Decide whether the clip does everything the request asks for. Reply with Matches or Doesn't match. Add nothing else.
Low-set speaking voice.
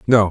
Matches